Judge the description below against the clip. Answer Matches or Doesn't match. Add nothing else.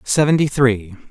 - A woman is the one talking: Doesn't match